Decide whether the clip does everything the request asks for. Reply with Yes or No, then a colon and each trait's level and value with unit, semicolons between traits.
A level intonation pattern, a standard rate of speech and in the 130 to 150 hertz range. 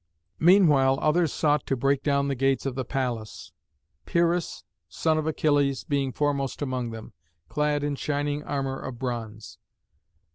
Yes: narrow, 2.2 semitones; average, 145 wpm; medium, 140 Hz